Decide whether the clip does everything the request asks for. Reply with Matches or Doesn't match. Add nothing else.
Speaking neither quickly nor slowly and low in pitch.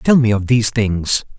Doesn't match